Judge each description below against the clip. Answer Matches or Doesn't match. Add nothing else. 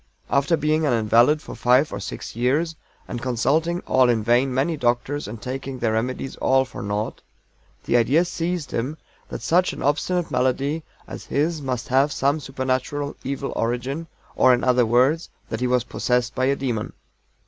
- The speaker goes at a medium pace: Matches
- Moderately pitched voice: Doesn't match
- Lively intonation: Doesn't match